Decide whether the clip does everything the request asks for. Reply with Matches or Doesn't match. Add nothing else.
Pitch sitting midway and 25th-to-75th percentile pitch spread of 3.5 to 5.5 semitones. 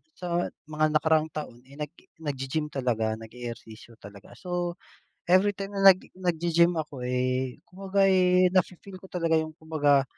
Matches